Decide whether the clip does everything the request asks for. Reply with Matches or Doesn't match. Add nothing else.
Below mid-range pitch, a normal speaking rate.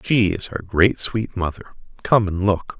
Matches